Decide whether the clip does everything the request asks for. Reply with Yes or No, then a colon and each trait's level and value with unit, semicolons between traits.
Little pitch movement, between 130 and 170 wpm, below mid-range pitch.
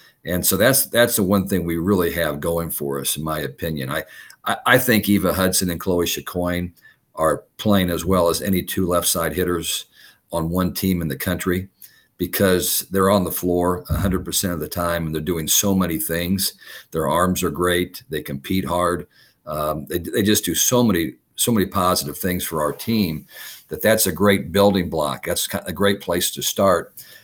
No: narrow, 2.3 semitones; average, 195 wpm; very low, 90 Hz